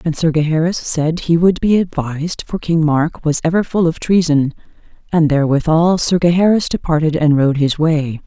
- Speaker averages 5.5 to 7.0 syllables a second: No, 5.1 syllables/s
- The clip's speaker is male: No, female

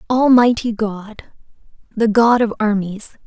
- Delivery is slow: Yes, slow, 110 wpm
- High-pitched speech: Yes, high, 220 Hz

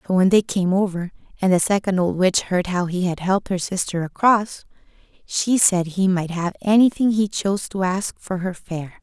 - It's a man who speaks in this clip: No, female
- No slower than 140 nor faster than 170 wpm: No, fast, 205 wpm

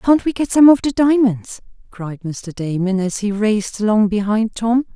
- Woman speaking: Yes, female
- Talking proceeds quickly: No, average, 195 wpm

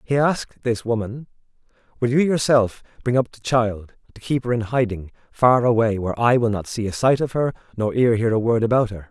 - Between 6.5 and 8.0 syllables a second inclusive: No, 5.5 syllables/s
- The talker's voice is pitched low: Yes, low, 115 Hz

